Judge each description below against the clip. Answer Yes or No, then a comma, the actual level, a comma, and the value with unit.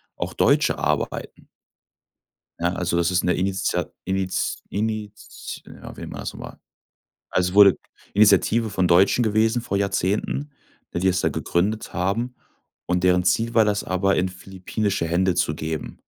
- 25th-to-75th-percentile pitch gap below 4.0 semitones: Yes, average, 2.8 semitones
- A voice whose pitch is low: Yes, very low, 95 Hz